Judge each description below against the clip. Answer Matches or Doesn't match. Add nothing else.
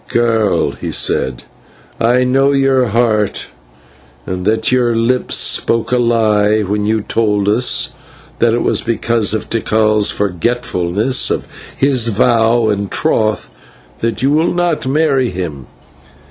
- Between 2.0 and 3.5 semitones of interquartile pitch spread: Matches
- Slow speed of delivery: Matches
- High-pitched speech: Doesn't match